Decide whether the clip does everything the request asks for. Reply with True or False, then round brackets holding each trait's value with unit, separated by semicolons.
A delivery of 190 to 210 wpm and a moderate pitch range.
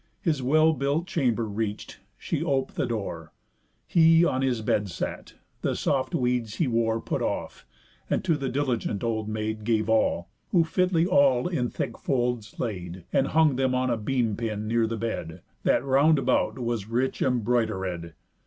False (170 wpm; 4.0 semitones)